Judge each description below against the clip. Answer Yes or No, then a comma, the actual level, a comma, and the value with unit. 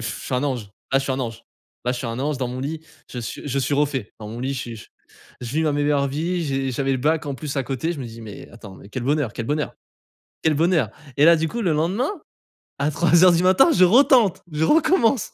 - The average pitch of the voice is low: No, medium, 145 Hz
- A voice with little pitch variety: No, average, 4.5 semitones